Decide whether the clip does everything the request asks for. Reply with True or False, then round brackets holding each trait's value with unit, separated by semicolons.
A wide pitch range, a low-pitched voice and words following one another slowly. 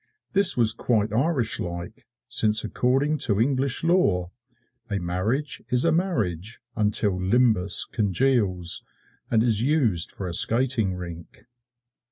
True (6.2 semitones; 110 Hz; 125 wpm)